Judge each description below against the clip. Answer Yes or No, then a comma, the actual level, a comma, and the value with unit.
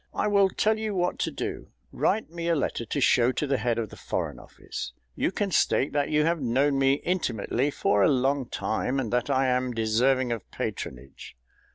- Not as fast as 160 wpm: No, fast, 205 wpm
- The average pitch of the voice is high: No, low, 135 Hz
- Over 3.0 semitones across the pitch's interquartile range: Yes, average, 5.3 semitones